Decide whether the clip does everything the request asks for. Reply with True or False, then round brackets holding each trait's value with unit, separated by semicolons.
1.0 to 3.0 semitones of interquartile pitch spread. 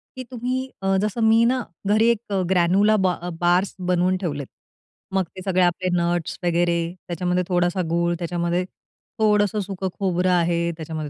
True (2.4 semitones)